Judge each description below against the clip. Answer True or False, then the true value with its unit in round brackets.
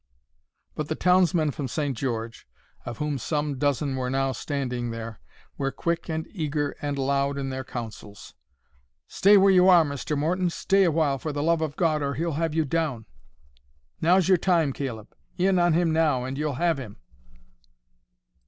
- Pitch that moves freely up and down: False (3.7 semitones)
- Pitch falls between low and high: True (150 Hz)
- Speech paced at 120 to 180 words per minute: True (165 wpm)